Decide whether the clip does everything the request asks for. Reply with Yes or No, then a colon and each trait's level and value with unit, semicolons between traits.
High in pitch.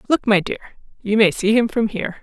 Yes: high, 215 Hz